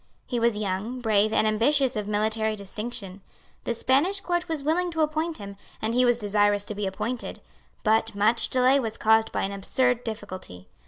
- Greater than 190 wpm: No, average, 180 wpm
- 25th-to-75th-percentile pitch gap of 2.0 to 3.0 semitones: No, average, 3.6 semitones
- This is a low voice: No, high, 220 Hz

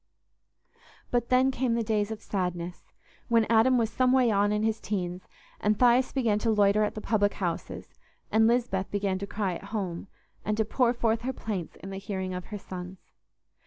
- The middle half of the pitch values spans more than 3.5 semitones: No, average, 3.2 semitones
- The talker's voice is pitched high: Yes, high, 210 Hz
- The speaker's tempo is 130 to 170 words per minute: No, average, 190 wpm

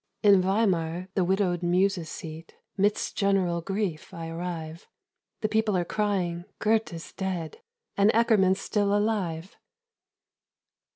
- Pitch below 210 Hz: Yes, high, 190 Hz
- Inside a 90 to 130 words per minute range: Yes, slow, 115 wpm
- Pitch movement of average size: Yes, average, 3.2 semitones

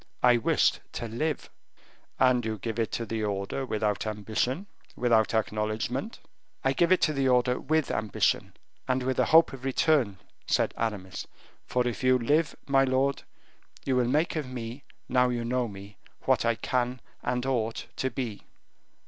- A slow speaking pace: No, average, 165 wpm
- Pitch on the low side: Yes, low, 125 Hz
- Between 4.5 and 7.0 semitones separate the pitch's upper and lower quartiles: No, average, 3.1 semitones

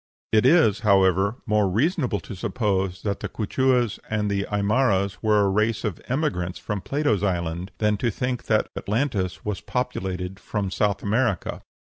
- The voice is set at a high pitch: No, low, 105 Hz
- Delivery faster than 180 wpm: No, average, 150 wpm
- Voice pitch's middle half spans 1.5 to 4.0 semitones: Yes, average, 3.4 semitones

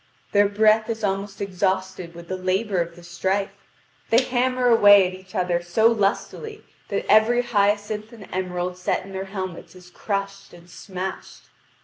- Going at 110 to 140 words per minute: No, average, 160 wpm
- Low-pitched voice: No, high, 195 Hz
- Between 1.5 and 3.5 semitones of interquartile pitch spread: Yes, average, 2.7 semitones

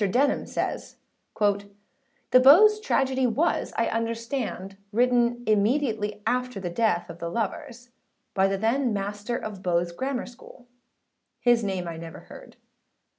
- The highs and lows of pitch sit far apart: No, average, 4.1 semitones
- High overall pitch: Yes, high, 230 Hz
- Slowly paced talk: Yes, slow, 130 wpm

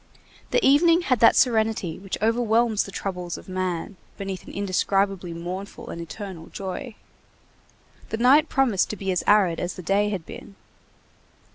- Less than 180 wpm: Yes, average, 155 wpm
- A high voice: Yes, high, 195 Hz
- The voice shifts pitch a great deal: No, average, 3.6 semitones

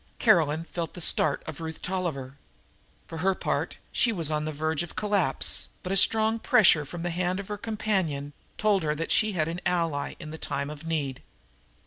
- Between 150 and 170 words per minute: No, average, 195 wpm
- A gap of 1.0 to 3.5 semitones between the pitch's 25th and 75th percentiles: No, average, 3.9 semitones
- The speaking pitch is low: No, medium, 165 Hz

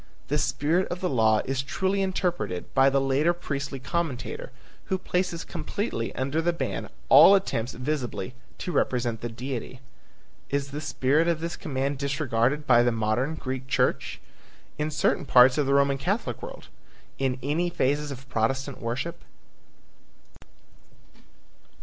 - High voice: No, medium, 140 Hz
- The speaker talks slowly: No, average, 145 wpm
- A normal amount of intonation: Yes, average, 4.7 semitones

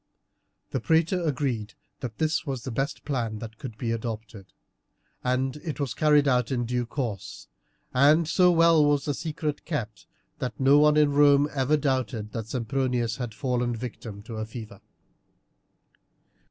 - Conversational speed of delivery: Yes, average, 155 wpm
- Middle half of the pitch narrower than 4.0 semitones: No, average, 4.3 semitones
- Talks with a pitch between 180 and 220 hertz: No, low, 130 Hz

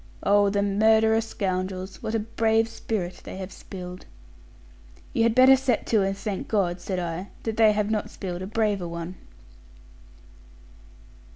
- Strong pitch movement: No, average, 3.0 semitones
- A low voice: No, high, 205 Hz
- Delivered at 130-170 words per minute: Yes, average, 155 wpm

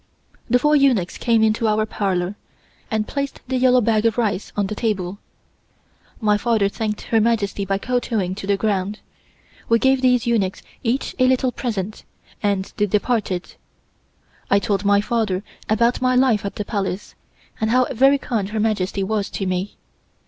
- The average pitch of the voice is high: Yes, high, 215 Hz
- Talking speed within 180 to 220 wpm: No, average, 170 wpm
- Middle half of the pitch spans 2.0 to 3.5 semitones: Yes, average, 3.2 semitones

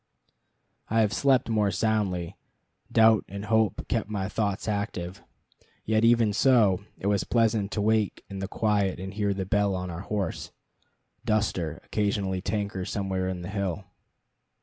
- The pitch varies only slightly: Yes, narrow, 2.3 semitones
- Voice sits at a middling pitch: No, low, 100 Hz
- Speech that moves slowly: No, average, 150 wpm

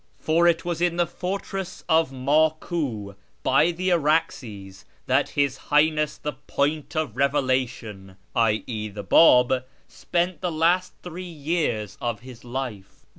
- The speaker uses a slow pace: Yes, slow, 130 wpm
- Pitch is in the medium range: Yes, medium, 145 Hz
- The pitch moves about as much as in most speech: No, wide, 5.7 semitones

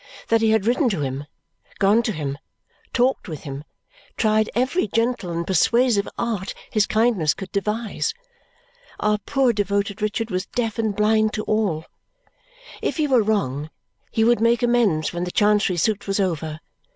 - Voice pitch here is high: Yes, high, 210 Hz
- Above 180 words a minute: No, average, 165 wpm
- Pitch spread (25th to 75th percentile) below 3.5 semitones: No, average, 3.9 semitones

